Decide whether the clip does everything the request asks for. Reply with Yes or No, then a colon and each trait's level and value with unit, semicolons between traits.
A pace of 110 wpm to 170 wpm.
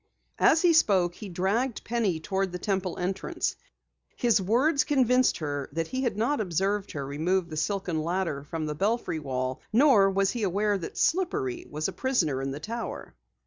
No: average, 180 wpm